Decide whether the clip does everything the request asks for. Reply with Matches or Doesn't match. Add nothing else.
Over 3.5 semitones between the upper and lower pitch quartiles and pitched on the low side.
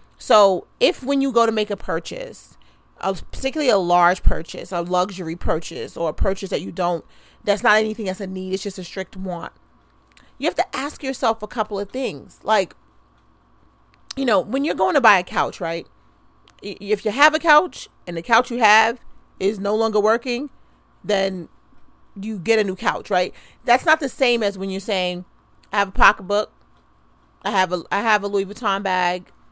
Doesn't match